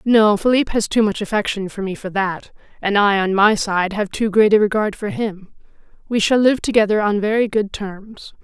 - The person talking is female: Yes, female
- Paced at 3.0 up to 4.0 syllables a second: No, 5.0 syllables/s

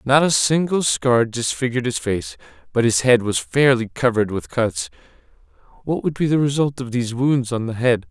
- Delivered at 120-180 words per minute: No, average, 195 wpm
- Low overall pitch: Yes, low, 125 Hz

